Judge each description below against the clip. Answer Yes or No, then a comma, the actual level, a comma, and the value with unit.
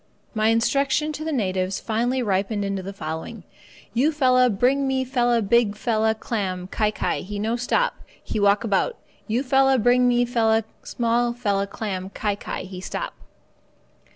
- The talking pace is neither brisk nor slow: Yes, average, 155 wpm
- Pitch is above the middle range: Yes, high, 225 Hz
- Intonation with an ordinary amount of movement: Yes, average, 3.8 semitones